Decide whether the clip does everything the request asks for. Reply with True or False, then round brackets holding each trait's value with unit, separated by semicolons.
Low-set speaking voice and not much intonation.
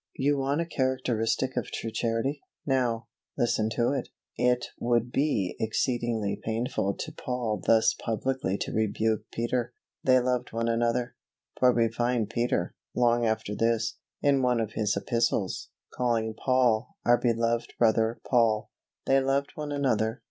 True (120 Hz; 2.2 semitones)